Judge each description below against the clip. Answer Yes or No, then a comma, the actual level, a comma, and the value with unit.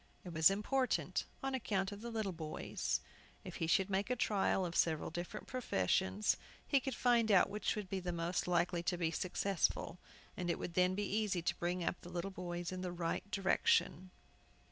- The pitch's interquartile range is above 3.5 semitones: No, average, 3.1 semitones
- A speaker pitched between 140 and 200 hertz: Yes, medium, 185 Hz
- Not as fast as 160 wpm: No, average, 195 wpm